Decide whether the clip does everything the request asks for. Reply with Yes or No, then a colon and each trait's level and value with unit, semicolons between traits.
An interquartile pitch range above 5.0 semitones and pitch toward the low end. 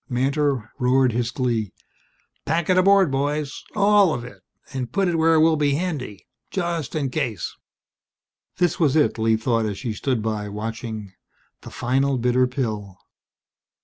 Yes: wide, 5.4 semitones; low, 130 Hz